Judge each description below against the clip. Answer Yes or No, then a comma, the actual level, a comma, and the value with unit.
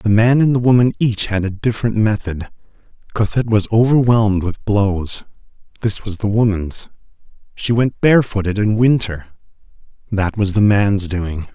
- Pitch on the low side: Yes, low, 105 Hz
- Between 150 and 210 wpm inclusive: No, average, 140 wpm